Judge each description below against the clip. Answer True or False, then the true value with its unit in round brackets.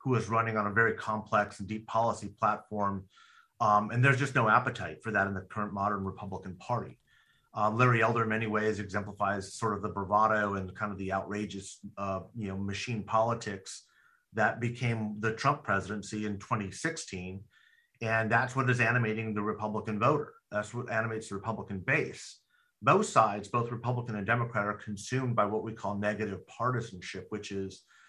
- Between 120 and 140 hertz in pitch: False (105 Hz)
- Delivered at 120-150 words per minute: False (175 wpm)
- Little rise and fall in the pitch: True (2.3 semitones)